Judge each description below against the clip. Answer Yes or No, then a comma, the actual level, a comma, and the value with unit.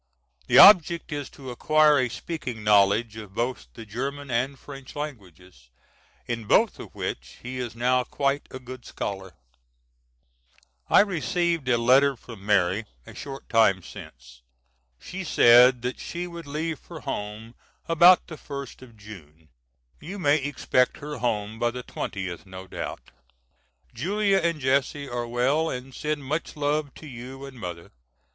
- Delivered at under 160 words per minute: Yes, average, 150 wpm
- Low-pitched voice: Yes, low, 125 Hz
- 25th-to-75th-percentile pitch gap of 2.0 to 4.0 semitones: No, average, 5.2 semitones